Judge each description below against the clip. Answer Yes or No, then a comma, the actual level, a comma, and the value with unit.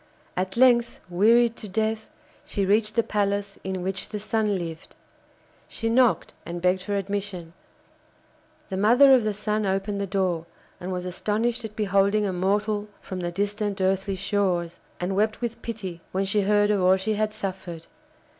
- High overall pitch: Yes, high, 200 Hz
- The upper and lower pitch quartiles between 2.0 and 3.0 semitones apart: Yes, narrow, 2.4 semitones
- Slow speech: No, average, 170 wpm